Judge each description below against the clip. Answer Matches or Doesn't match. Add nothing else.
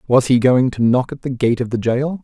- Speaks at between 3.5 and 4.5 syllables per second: Doesn't match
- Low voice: Matches